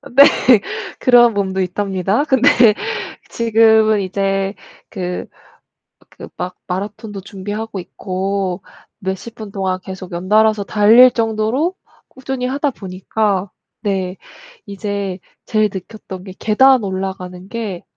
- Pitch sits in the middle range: No, high, 200 Hz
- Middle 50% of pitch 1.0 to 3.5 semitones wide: Yes, average, 2.7 semitones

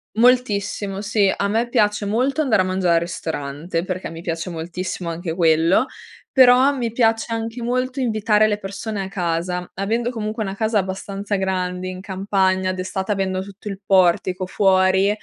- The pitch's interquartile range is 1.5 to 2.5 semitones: No, average, 2.9 semitones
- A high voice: Yes, high, 195 Hz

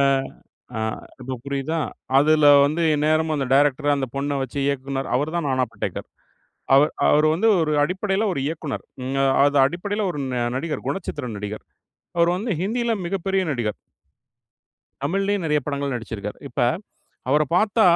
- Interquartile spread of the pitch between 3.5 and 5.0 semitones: Yes, average, 4.1 semitones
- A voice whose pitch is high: No, medium, 150 Hz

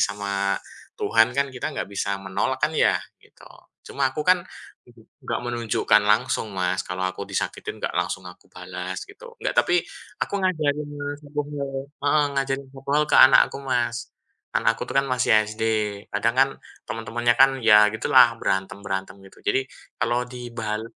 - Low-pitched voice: Yes, low, 115 Hz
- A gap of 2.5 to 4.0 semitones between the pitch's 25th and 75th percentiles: No, average, 5.2 semitones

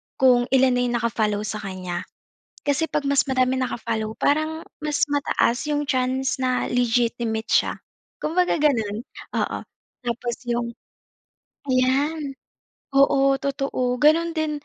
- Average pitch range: Yes, average, 3.4 semitones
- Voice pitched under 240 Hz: No, very high, 255 Hz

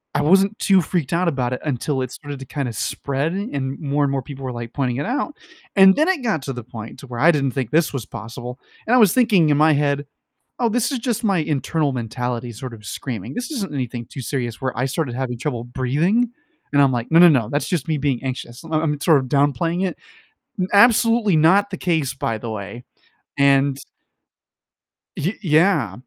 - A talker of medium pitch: Yes, medium, 145 Hz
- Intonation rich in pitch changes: Yes, wide, 5.7 semitones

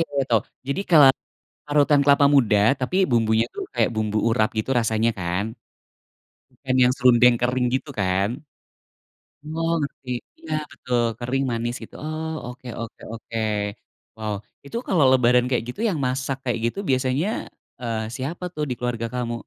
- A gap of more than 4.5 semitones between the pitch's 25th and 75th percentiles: No, average, 3.5 semitones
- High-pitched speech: No, low, 125 Hz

